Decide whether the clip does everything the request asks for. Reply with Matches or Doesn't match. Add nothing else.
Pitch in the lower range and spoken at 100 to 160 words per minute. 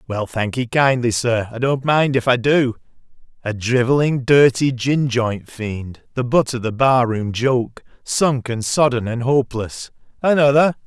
Matches